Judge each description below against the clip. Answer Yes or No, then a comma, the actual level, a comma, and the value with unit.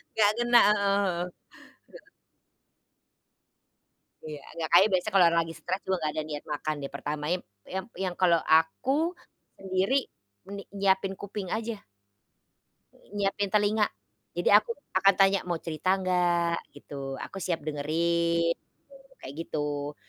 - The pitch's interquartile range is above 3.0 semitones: Yes, average, 3.8 semitones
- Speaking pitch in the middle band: Yes, medium, 180 Hz